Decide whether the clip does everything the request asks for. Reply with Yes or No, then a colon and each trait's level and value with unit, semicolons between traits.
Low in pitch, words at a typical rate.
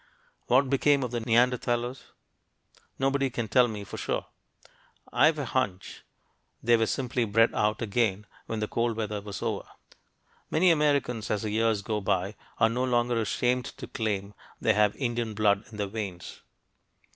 Yes: low, 115 Hz; average, 160 wpm